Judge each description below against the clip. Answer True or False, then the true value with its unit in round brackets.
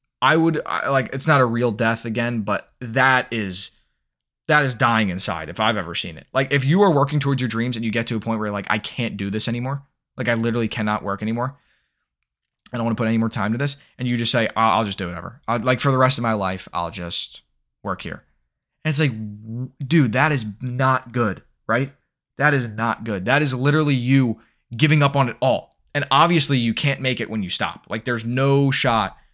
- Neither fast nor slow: False (240 wpm)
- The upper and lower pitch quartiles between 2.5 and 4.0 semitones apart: True (3.7 semitones)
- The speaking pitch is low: True (120 Hz)